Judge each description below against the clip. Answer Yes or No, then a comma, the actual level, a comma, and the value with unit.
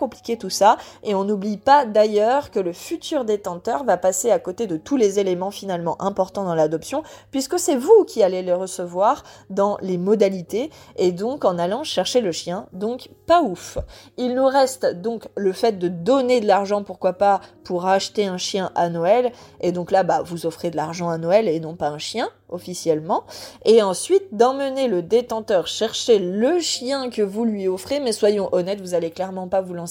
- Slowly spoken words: No, average, 200 wpm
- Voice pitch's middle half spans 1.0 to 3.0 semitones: No, average, 5.3 semitones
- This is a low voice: No, high, 200 Hz